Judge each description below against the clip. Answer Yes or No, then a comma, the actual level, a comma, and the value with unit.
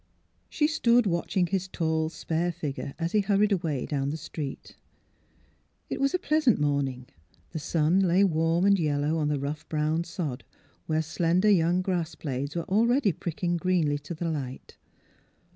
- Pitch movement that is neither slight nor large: Yes, average, 4.0 semitones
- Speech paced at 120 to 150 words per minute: No, average, 160 wpm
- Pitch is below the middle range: No, medium, 165 Hz